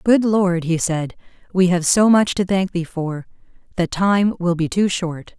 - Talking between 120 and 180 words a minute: No, average, 200 wpm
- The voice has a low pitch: No, medium, 180 Hz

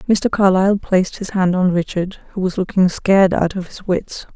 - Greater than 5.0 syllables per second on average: Yes, 5.3 syllables/s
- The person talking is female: Yes, female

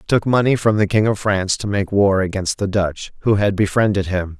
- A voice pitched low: Yes, low, 100 Hz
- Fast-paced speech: Yes, fast, 245 wpm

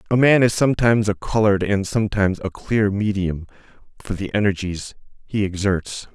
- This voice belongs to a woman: No, male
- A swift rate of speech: No, average, 155 wpm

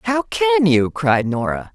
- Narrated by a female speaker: Yes, female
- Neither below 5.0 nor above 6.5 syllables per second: No, 3.8 syllables/s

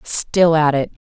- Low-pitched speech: No, medium, 160 Hz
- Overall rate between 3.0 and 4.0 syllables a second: Yes, 3.6 syllables/s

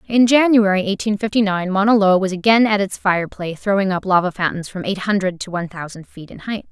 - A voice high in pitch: Yes, high, 195 Hz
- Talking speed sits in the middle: No, fast, 230 wpm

